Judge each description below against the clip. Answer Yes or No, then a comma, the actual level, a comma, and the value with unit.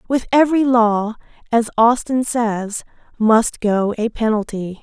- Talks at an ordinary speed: No, slow, 125 wpm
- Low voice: No, high, 225 Hz